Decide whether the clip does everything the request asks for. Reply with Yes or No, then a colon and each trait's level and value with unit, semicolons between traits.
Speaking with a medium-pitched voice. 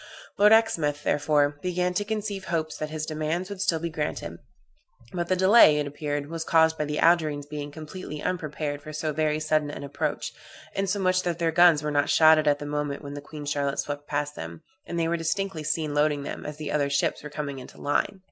Yes: medium, 155 Hz